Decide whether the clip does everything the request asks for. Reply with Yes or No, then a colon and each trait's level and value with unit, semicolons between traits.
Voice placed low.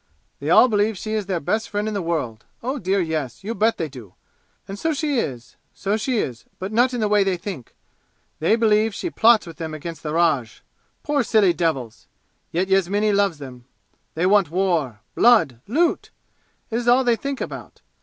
No: high, 195 Hz